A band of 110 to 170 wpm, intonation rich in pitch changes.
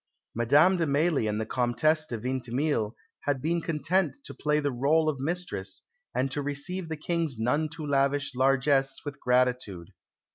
No: average, 160 wpm; average, 3.7 semitones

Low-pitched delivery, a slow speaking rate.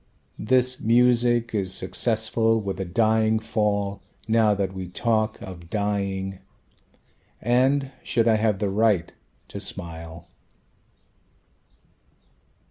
Yes: low, 110 Hz; slow, 105 wpm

